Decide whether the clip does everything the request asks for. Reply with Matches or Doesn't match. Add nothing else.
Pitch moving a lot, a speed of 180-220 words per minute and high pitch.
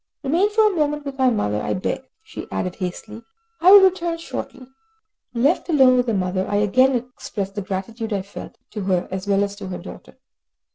Matches